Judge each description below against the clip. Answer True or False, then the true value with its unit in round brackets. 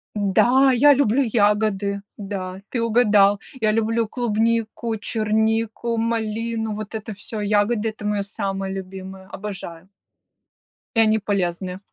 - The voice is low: False (215 Hz)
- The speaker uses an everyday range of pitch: False (2.2 semitones)